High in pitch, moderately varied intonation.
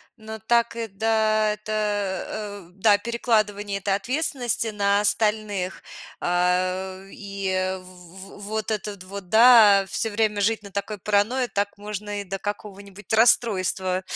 No: high, 205 Hz; narrow, 2.0 semitones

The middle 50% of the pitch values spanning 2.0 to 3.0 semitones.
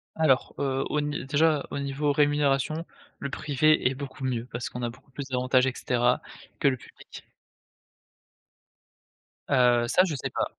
Yes: narrow, 2.5 semitones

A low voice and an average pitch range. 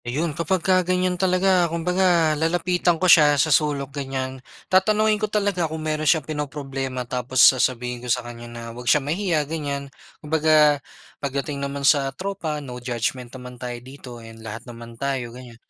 No: medium, 145 Hz; average, 4.9 semitones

